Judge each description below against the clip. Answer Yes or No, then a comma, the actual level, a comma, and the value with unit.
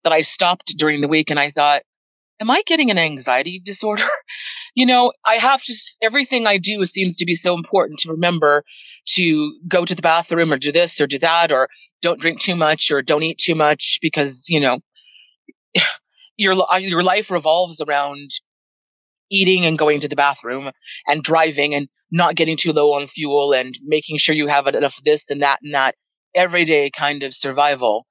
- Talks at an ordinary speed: Yes, average, 190 wpm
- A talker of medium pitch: Yes, medium, 160 Hz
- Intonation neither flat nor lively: Yes, average, 3.8 semitones